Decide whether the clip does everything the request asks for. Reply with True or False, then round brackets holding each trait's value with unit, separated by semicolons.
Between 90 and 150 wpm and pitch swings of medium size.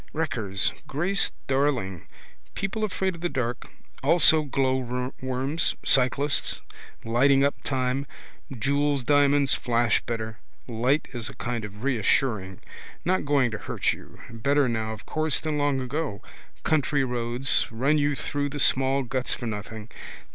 True (135 wpm; 3.4 semitones)